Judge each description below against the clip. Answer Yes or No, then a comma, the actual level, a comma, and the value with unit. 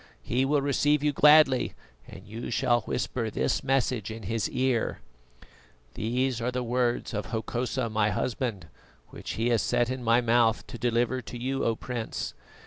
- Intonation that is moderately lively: No, narrow, 2.3 semitones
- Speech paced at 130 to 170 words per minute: Yes, average, 165 wpm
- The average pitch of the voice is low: Yes, low, 120 Hz